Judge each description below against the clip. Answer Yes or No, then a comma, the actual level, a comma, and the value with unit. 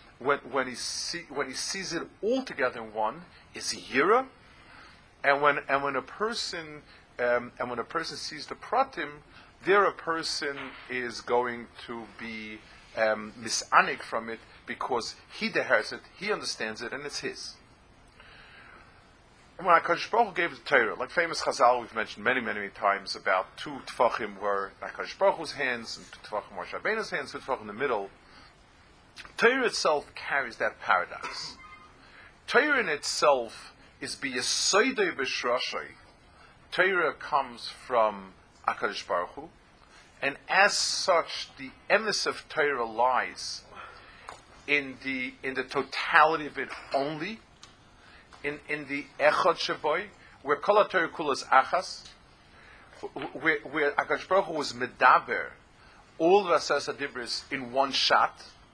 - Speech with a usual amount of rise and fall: No, wide, 5.7 semitones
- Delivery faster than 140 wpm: No, slow, 135 wpm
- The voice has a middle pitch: No, low, 130 Hz